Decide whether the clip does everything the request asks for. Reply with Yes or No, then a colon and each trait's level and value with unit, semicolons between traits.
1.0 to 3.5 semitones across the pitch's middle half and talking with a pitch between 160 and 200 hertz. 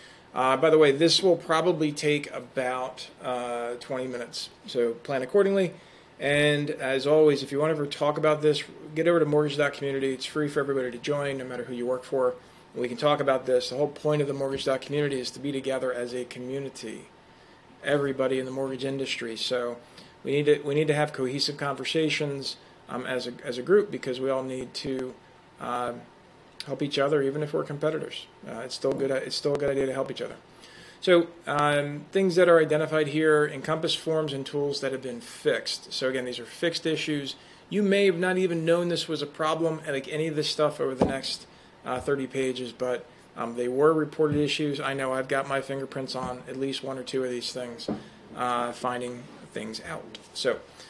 No: average, 2.9 semitones; medium, 140 Hz